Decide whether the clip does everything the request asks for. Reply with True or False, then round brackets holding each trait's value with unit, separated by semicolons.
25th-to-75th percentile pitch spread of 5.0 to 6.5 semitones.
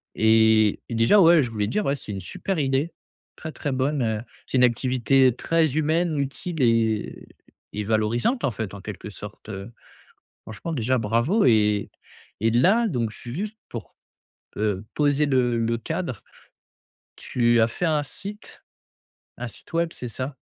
True (5.5 semitones)